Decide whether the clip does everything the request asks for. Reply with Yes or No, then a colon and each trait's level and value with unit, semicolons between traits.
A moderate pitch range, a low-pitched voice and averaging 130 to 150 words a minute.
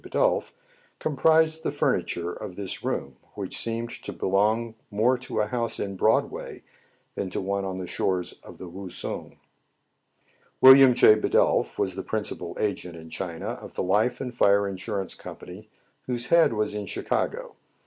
No: average, 4.0 semitones; low, 105 Hz; average, 160 wpm